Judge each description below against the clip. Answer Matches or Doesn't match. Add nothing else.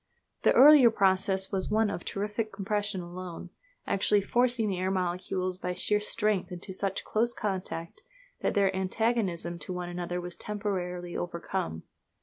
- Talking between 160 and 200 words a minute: Doesn't match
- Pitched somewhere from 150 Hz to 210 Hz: Matches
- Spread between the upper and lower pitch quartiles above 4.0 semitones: Doesn't match